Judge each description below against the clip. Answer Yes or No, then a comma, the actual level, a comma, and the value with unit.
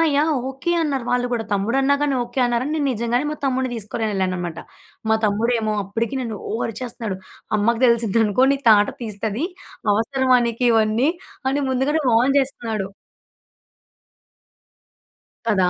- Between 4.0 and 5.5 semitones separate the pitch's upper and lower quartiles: No, average, 3.4 semitones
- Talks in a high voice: Yes, high, 235 Hz